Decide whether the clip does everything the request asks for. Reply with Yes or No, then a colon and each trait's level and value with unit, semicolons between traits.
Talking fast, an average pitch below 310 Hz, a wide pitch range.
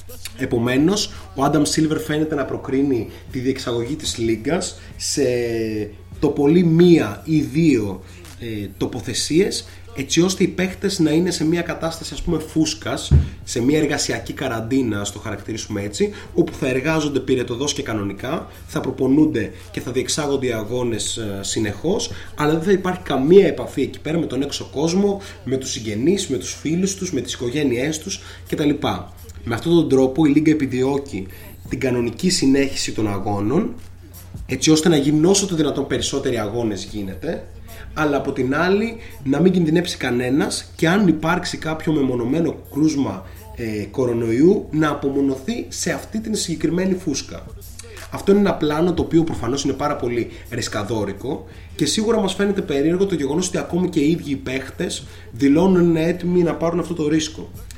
No: average, 160 wpm; low, 135 Hz; wide, 7.5 semitones